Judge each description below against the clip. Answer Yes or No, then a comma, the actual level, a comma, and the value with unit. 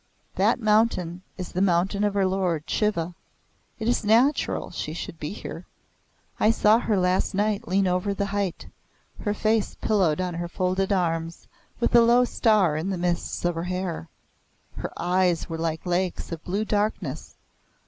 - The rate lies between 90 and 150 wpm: No, average, 170 wpm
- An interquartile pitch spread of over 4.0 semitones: No, average, 3.2 semitones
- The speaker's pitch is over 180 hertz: Yes, high, 190 Hz